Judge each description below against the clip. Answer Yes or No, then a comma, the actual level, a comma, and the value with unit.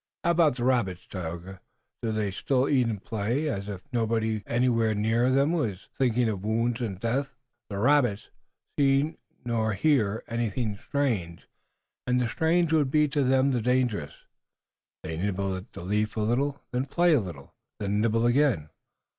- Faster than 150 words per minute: Yes, average, 170 wpm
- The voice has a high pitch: No, low, 115 Hz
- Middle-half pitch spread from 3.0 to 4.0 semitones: No, average, 4.8 semitones